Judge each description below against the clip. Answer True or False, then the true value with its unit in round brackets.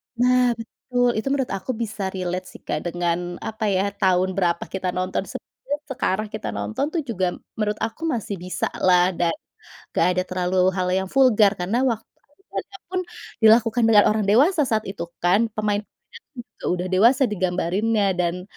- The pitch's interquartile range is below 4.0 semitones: False (4.3 semitones)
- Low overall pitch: False (200 Hz)